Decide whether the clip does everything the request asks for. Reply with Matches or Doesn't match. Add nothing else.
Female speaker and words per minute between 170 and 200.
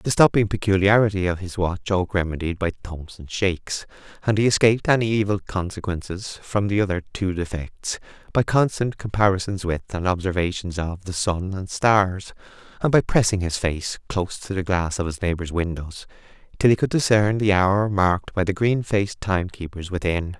Doesn't match